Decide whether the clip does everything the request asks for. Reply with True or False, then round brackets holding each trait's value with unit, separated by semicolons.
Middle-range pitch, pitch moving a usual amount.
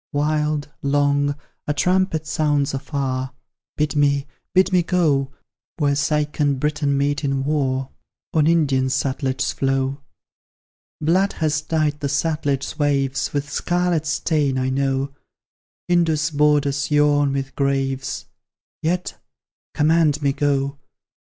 False (145 Hz; 1.9 semitones)